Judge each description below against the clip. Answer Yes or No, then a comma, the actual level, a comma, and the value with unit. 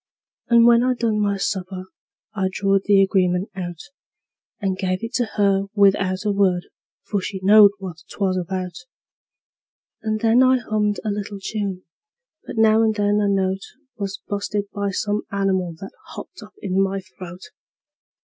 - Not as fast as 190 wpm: Yes, average, 160 wpm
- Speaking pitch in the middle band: No, high, 200 Hz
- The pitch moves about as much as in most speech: No, narrow, 1.8 semitones